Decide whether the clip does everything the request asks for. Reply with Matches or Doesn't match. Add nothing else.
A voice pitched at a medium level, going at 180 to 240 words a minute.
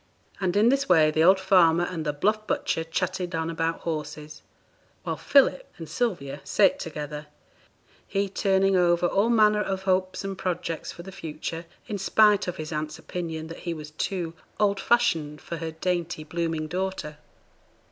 Doesn't match